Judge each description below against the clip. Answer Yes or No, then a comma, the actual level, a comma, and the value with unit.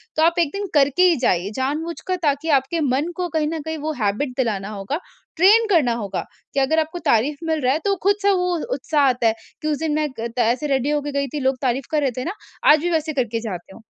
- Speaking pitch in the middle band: No, very high, 290 Hz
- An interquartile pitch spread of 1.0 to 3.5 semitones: No, average, 4.2 semitones